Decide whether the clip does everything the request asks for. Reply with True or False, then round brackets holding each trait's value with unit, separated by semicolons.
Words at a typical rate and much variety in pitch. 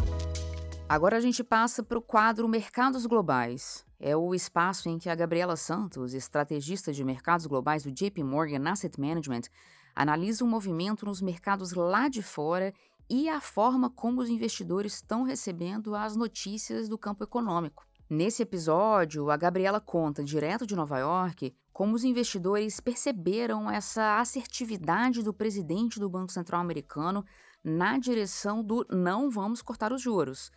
True (150 wpm; 6.1 semitones)